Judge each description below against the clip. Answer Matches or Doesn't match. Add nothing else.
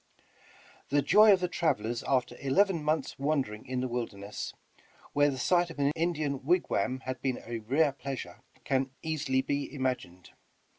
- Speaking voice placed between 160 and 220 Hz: Doesn't match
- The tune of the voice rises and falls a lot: Doesn't match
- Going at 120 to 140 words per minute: Doesn't match